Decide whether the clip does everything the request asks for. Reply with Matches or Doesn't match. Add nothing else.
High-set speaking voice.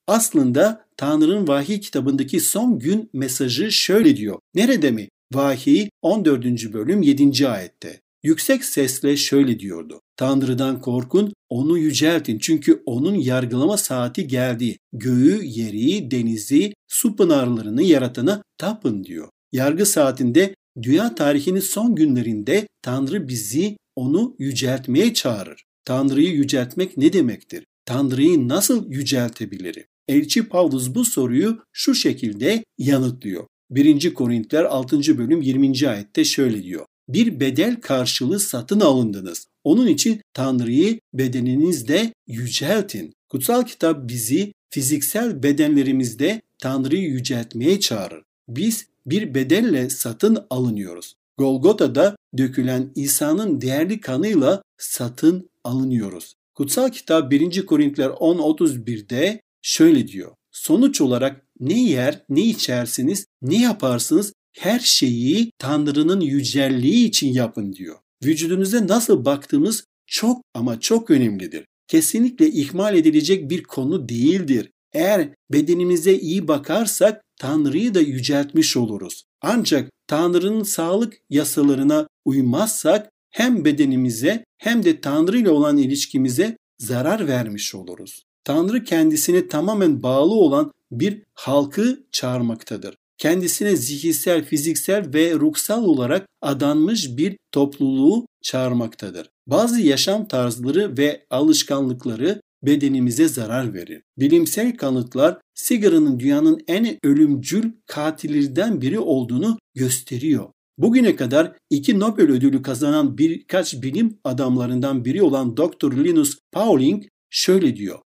Doesn't match